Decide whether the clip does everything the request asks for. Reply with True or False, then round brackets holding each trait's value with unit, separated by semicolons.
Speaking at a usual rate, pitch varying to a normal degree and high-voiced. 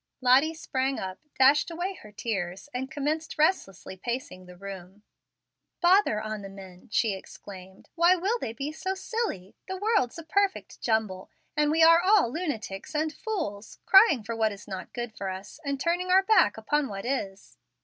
False (175 wpm; 8.9 semitones; 260 Hz)